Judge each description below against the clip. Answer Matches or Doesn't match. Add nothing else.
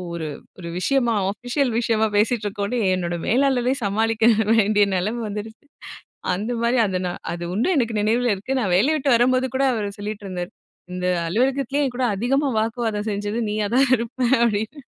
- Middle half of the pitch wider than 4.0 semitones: Doesn't match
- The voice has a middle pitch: Doesn't match